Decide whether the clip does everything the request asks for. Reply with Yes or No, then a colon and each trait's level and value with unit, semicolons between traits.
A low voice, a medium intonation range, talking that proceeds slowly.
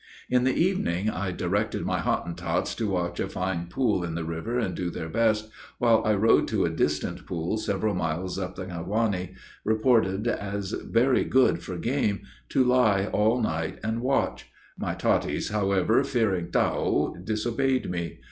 No: low, 105 Hz; average, 4.2 semitones; average, 165 wpm